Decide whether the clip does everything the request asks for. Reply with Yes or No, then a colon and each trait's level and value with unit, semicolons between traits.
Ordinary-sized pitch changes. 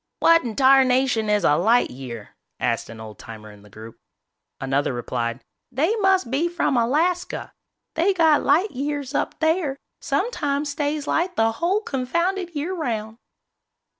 No: wide, 8.0 semitones